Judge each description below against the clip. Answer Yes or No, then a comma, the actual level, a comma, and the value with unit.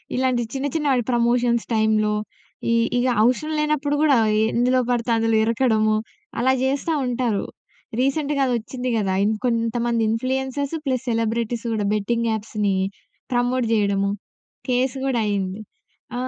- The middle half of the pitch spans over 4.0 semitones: No, average, 2.9 semitones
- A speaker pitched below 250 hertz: Yes, high, 240 Hz